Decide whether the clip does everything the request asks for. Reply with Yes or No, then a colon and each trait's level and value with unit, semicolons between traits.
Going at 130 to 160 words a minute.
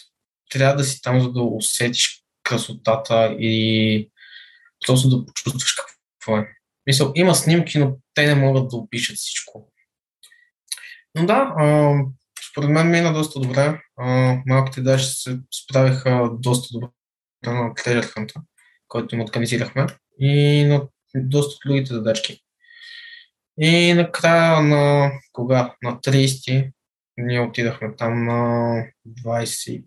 No: slow, 115 wpm